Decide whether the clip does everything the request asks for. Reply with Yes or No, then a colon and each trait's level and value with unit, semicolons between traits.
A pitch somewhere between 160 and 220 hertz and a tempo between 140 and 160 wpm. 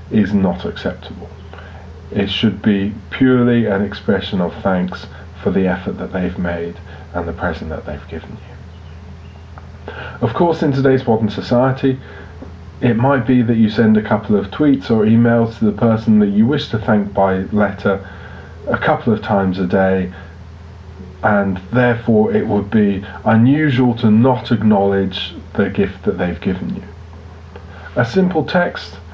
No: low, 100 Hz; average, 155 wpm